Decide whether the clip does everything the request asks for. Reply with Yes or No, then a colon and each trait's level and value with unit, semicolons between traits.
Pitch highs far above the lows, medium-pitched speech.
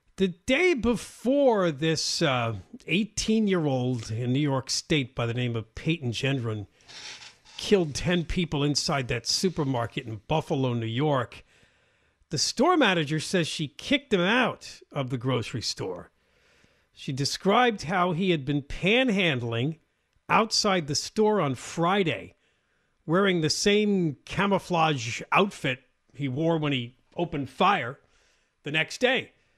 Yes: wide, 7.0 semitones; medium, 155 Hz